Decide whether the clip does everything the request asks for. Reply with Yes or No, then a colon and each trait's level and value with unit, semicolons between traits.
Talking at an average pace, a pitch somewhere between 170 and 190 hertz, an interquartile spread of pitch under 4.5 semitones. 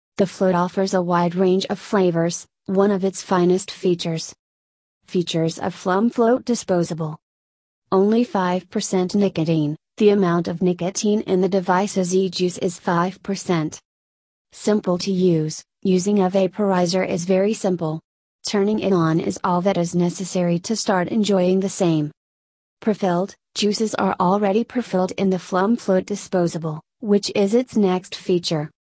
Yes: average, 145 wpm; medium, 185 Hz; narrow, 2.4 semitones